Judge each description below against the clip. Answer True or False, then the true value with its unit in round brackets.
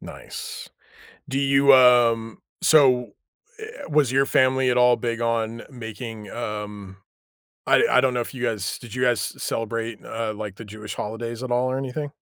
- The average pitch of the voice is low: True (120 Hz)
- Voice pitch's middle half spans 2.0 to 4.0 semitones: True (2.5 semitones)